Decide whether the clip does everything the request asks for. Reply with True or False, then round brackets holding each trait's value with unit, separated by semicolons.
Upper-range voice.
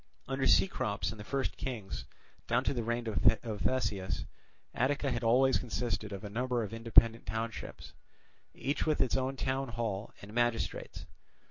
False (120 Hz)